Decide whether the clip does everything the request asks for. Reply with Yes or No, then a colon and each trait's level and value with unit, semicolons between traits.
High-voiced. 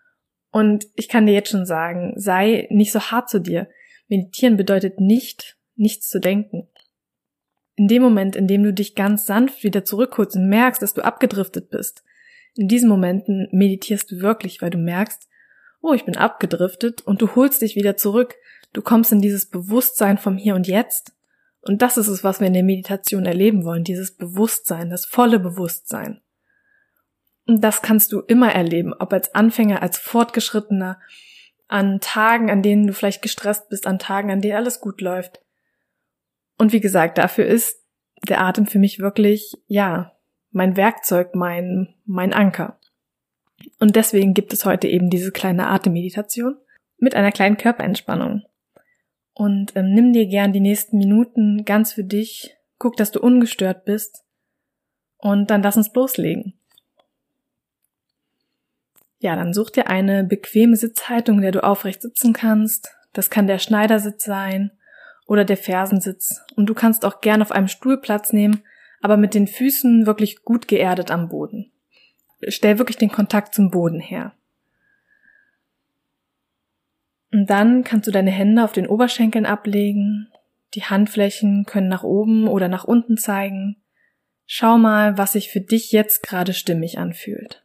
Yes: high, 210 Hz